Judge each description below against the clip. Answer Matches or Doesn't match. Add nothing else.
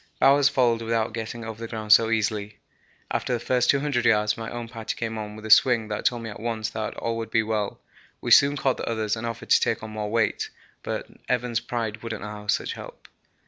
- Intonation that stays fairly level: Matches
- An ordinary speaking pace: Doesn't match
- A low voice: Matches